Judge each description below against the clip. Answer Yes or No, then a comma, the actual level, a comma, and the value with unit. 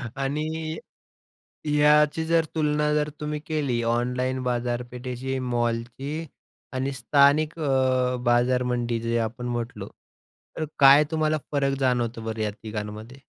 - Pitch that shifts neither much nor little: Yes, average, 3.6 semitones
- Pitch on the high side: No, low, 130 Hz